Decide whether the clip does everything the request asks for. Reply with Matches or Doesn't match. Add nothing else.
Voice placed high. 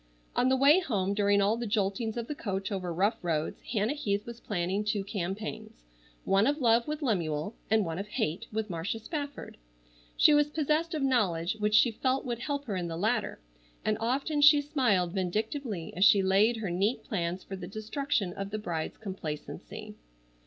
Matches